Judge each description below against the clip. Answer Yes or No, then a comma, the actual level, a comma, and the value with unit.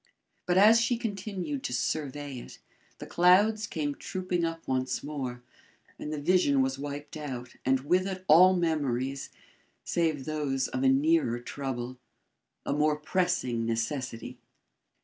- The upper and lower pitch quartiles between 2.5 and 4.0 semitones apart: No, average, 5.2 semitones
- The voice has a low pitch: No, medium, 145 Hz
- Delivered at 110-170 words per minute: Yes, average, 140 wpm